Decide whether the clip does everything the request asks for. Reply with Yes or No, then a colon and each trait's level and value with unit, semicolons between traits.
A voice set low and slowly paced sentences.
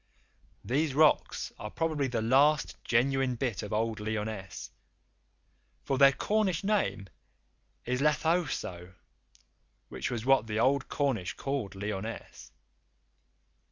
Yes: low, 130 Hz; slow, 110 wpm